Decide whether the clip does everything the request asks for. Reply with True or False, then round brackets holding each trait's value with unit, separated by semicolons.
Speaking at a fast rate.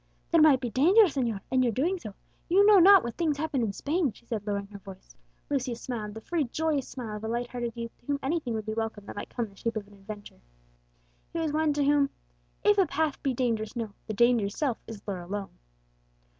True (235 wpm)